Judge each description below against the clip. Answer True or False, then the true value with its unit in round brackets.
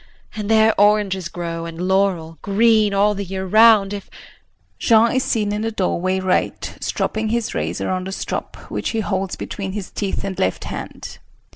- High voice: True (195 Hz)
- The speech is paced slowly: False (175 wpm)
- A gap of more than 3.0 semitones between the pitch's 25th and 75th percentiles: False (2.6 semitones)